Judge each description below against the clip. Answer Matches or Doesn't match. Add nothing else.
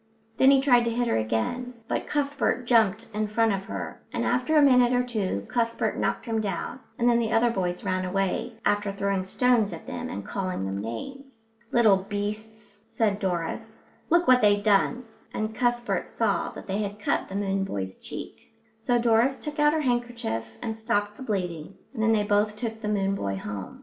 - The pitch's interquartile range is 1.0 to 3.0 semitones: Doesn't match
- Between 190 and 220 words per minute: Matches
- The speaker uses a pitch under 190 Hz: Doesn't match